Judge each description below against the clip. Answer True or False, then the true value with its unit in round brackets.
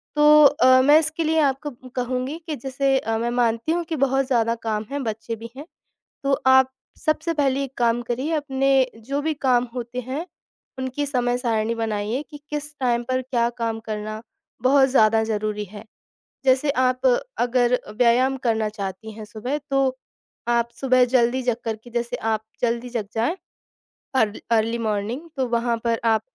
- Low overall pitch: False (245 Hz)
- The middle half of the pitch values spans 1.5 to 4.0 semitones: True (3.0 semitones)